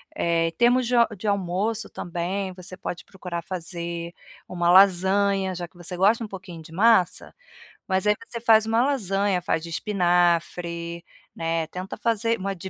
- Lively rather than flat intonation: No, average, 3.1 semitones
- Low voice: No, medium, 185 Hz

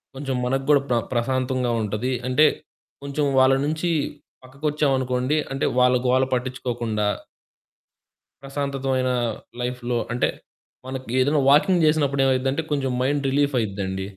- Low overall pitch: Yes, low, 130 Hz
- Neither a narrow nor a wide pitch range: No, narrow, 2.1 semitones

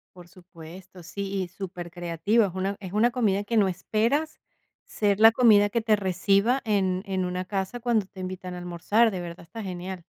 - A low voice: No, high, 190 Hz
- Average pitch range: Yes, average, 3.0 semitones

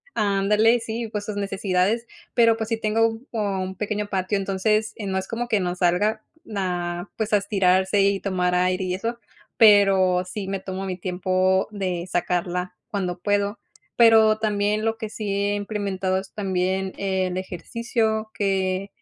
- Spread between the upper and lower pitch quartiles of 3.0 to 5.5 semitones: No, narrow, 2.4 semitones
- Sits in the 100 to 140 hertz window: No, high, 195 Hz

